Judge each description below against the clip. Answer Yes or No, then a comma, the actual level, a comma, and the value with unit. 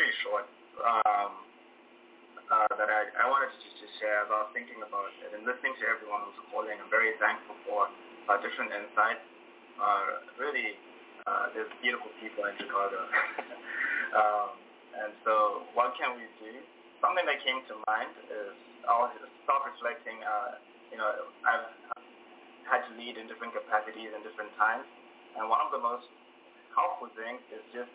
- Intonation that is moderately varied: Yes, average, 3.4 semitones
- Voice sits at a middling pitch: No, low, 115 Hz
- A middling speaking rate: Yes, average, 160 wpm